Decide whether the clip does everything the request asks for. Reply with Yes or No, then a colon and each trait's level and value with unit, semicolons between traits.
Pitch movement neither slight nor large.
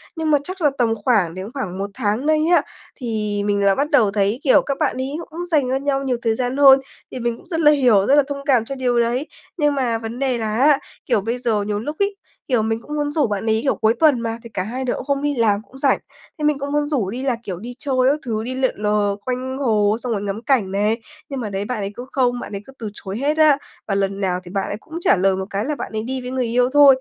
Yes: average, 4.8 semitones